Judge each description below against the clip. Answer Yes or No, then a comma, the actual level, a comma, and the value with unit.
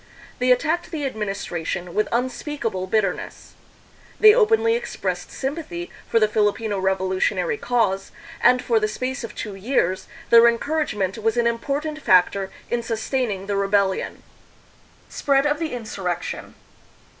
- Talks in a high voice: Yes, high, 230 Hz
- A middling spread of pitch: No, wide, 5.8 semitones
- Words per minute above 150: No, slow, 135 wpm